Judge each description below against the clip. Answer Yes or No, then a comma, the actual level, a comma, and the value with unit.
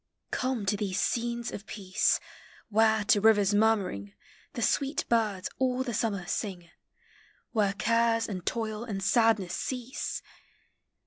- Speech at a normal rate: No, slow, 130 wpm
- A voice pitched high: Yes, high, 220 Hz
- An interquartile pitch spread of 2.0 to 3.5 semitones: Yes, average, 2.8 semitones